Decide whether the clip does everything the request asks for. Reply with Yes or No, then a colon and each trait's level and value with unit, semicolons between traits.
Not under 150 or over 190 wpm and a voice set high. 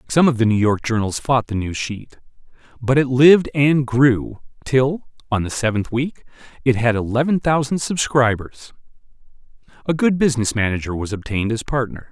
No: average, 165 wpm; low, 125 Hz